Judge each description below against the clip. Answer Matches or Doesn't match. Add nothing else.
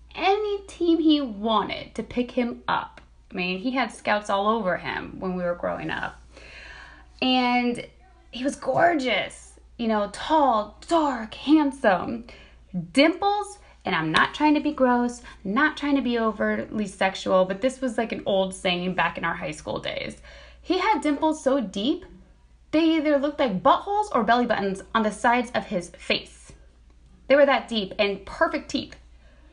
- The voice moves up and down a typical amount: Doesn't match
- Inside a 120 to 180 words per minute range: Matches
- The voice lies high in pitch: Matches